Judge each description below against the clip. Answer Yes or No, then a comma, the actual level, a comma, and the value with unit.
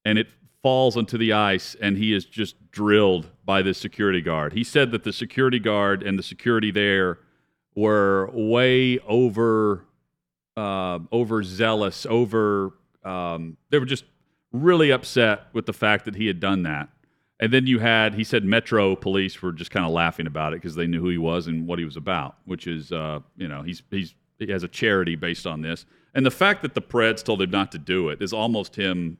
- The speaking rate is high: Yes, fast, 210 wpm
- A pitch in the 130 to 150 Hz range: No, low, 105 Hz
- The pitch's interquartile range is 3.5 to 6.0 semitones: Yes, average, 4.4 semitones